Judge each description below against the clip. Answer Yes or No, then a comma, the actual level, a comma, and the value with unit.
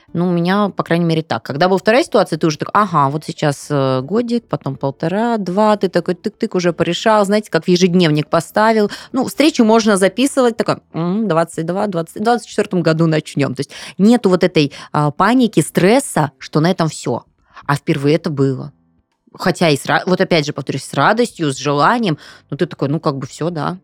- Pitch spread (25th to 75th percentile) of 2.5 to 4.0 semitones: No, wide, 5.4 semitones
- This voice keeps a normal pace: No, fast, 190 wpm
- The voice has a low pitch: No, medium, 170 Hz